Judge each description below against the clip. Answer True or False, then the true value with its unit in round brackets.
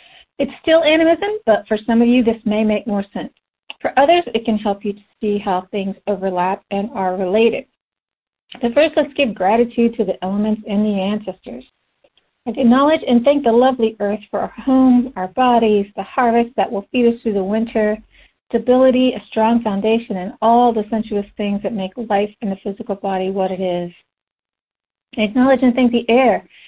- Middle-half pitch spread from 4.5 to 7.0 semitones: False (3.6 semitones)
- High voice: True (220 Hz)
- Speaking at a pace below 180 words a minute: False (185 wpm)